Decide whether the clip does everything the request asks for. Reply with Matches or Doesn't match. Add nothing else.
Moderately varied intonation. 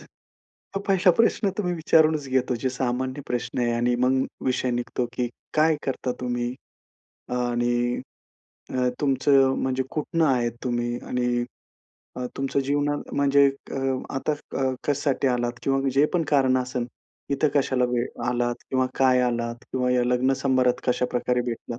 Doesn't match